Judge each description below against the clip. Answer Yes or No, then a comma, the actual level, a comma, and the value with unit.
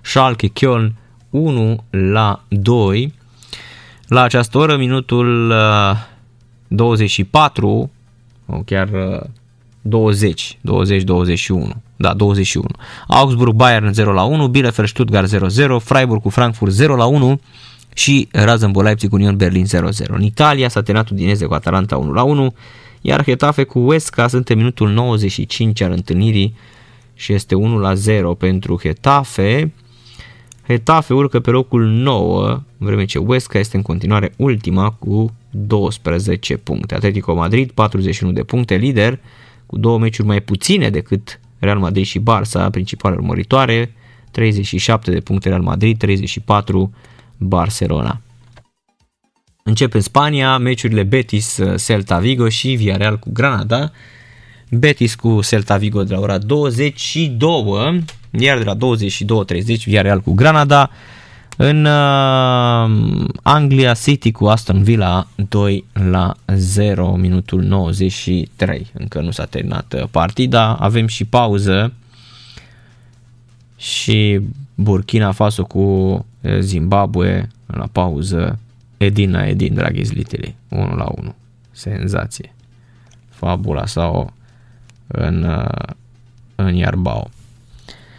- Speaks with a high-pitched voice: No, low, 115 Hz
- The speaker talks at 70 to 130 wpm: Yes, average, 120 wpm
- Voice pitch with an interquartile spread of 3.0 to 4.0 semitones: Yes, average, 3.6 semitones